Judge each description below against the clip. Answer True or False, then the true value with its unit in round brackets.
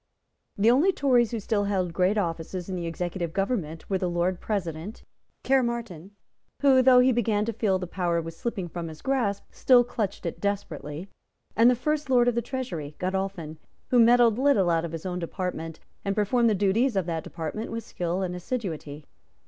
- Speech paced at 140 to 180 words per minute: False (190 wpm)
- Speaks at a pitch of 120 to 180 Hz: False (195 Hz)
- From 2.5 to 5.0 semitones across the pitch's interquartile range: False (5.6 semitones)